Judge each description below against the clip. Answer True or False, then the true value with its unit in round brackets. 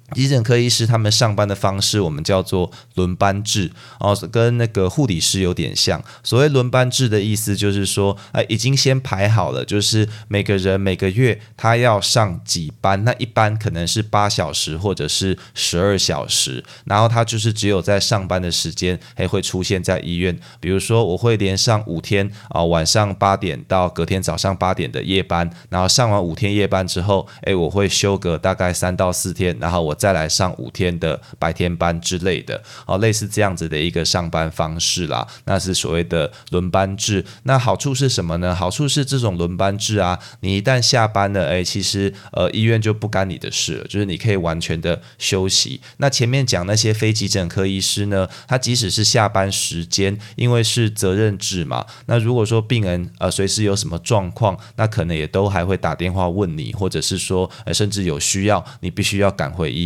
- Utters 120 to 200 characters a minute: False (300 characters per minute)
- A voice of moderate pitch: False (100 Hz)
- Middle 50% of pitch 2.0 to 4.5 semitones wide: True (3.3 semitones)